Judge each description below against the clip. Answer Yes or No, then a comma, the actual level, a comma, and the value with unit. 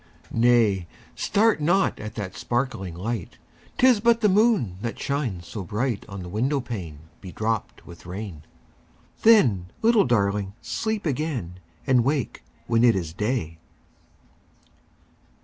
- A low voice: Yes, low, 115 Hz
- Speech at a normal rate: No, slow, 130 wpm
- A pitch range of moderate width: No, wide, 7.3 semitones